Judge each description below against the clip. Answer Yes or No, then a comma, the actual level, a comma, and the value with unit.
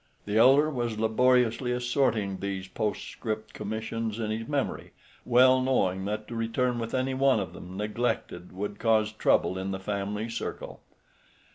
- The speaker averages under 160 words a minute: Yes, average, 150 wpm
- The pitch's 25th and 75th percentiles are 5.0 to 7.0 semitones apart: No, average, 3.2 semitones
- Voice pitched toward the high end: No, low, 110 Hz